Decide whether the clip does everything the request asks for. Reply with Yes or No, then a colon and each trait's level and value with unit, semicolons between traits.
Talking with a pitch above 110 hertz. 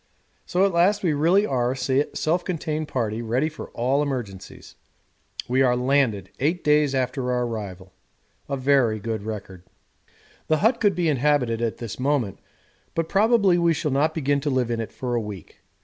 Yes: low, 135 Hz